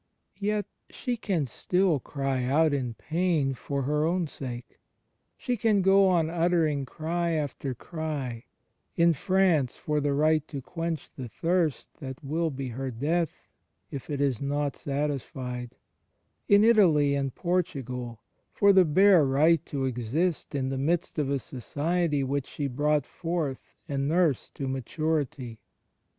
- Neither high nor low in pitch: Yes, medium, 150 Hz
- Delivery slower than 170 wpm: Yes, average, 145 wpm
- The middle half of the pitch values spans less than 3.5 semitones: No, average, 4.0 semitones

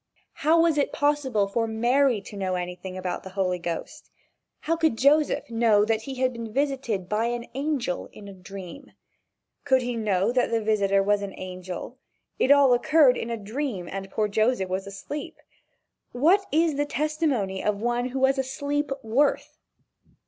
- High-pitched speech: Yes, high, 235 Hz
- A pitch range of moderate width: No, wide, 5.9 semitones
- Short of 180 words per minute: Yes, average, 170 wpm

